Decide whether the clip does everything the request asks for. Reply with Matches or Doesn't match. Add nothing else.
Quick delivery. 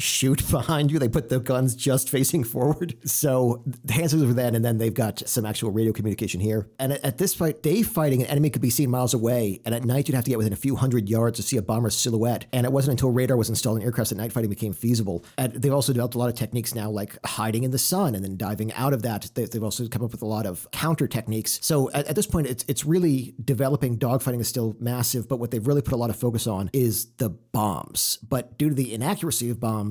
Matches